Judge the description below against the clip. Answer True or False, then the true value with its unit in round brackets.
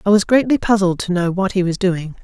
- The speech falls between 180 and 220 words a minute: False (270 wpm)